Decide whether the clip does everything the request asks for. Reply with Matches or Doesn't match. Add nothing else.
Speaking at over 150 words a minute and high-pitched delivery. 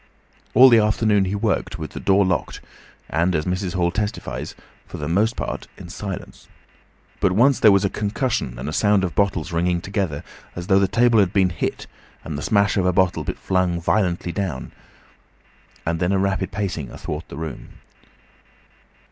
Doesn't match